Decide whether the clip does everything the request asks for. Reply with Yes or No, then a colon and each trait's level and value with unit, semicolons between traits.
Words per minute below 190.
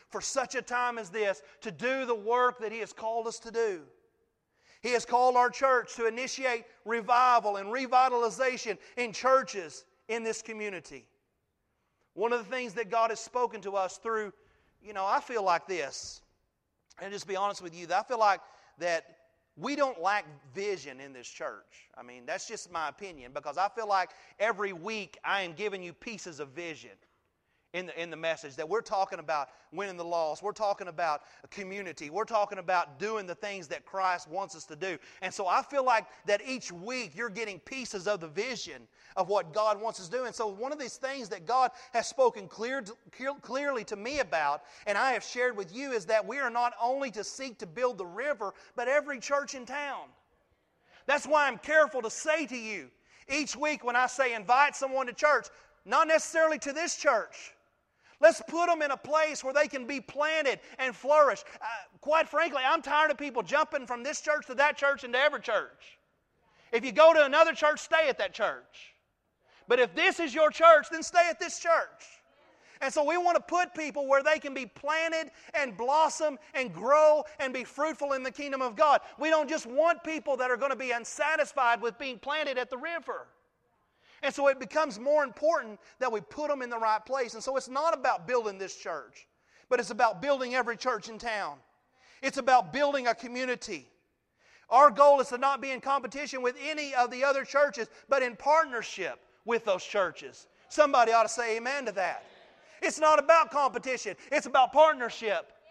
No: fast, 205 wpm